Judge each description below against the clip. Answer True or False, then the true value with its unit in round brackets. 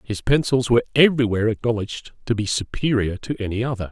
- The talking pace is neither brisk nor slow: True (170 wpm)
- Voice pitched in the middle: False (115 Hz)